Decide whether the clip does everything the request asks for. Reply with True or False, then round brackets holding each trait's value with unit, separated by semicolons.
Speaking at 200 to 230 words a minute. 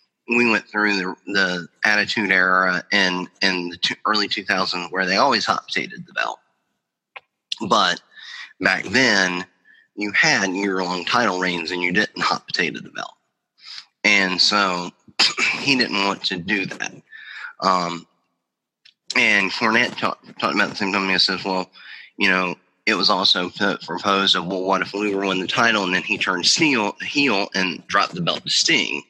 False (170 wpm)